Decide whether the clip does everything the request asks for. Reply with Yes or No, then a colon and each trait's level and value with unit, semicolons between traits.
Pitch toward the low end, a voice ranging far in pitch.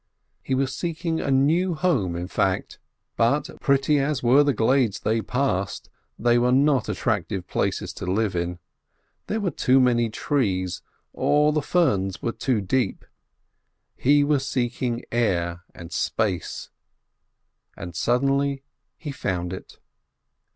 Yes: low, 125 Hz; wide, 6.4 semitones